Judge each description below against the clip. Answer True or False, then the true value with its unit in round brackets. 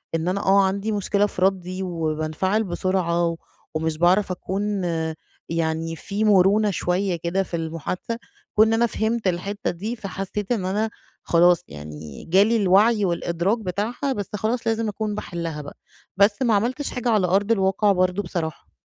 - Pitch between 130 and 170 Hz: False (195 Hz)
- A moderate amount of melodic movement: True (3.5 semitones)